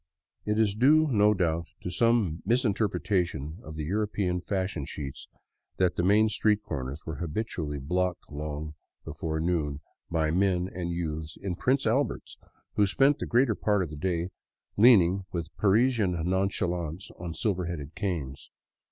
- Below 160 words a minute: Yes, average, 150 wpm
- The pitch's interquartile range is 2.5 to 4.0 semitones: No, average, 4.8 semitones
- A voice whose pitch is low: Yes, very low, 90 Hz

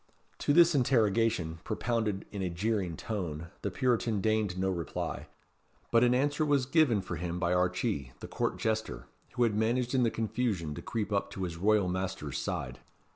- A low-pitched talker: Yes, low, 105 Hz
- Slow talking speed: No, average, 180 wpm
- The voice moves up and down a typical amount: Yes, average, 4.8 semitones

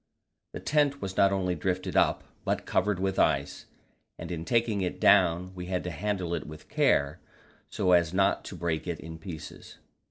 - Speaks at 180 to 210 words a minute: Yes, average, 185 wpm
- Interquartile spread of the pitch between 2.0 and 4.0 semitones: Yes, average, 2.9 semitones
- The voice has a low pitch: Yes, very low, 90 Hz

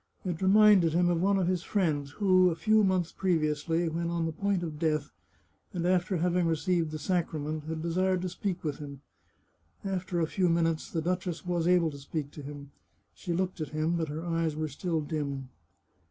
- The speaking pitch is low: No, medium, 170 Hz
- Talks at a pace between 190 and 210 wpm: Yes, average, 200 wpm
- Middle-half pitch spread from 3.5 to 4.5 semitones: No, average, 2.7 semitones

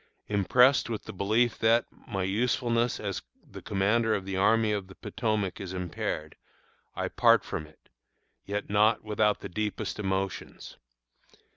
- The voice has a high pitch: No, low, 105 Hz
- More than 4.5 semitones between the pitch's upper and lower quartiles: No, average, 2.7 semitones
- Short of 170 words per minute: Yes, average, 145 wpm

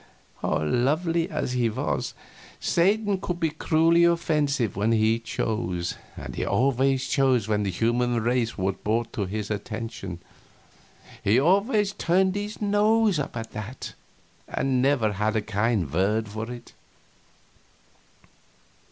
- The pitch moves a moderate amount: No, wide, 7.3 semitones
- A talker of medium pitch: No, low, 120 Hz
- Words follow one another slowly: Yes, slow, 130 wpm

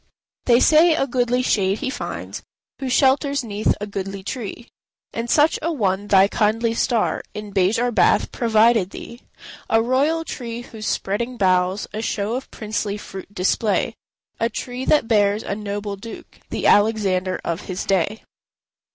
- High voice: Yes, high, 220 Hz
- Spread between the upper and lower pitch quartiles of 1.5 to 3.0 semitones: No, average, 3.5 semitones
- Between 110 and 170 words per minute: Yes, average, 155 wpm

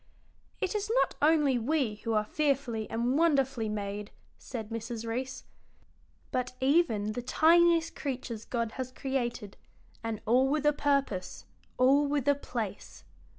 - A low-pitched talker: No, very high, 255 Hz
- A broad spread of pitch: No, average, 4.2 semitones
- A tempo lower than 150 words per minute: Yes, average, 140 wpm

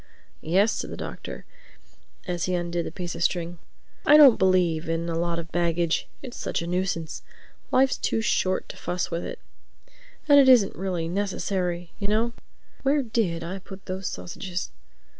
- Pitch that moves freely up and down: No, average, 3.1 semitones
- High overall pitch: No, medium, 180 Hz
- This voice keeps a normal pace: Yes, average, 165 wpm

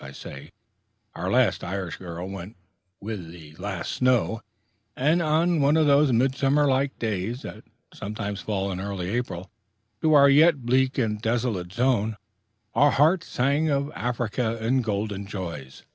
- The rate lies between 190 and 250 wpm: No, average, 150 wpm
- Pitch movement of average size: No, wide, 6.0 semitones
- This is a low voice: Yes, low, 115 Hz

